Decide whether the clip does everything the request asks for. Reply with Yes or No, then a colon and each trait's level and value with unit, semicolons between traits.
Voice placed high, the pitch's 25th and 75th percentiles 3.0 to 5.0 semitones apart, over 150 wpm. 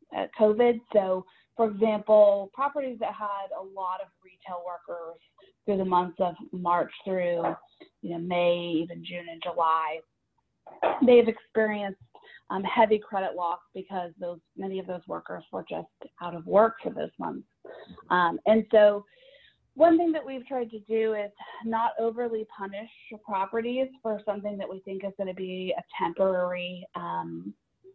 Yes: high, 195 Hz; average, 3.9 semitones; average, 160 wpm